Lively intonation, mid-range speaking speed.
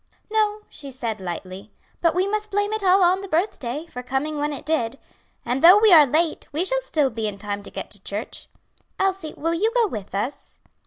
No: wide, 7.9 semitones; fast, 215 wpm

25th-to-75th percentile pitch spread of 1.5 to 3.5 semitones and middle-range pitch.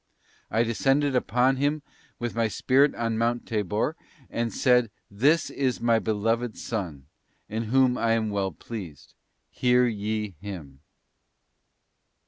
No: average, 2.9 semitones; low, 115 Hz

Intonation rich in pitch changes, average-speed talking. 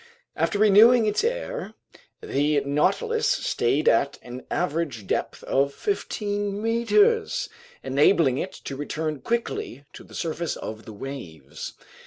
No: wide, 8.9 semitones; slow, 125 wpm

